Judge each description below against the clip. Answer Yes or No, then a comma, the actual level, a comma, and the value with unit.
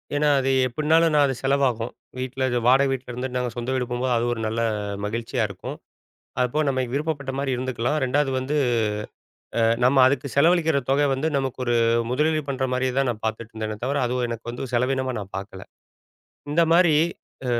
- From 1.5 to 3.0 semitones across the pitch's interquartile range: Yes, narrow, 2.6 semitones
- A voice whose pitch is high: No, low, 130 Hz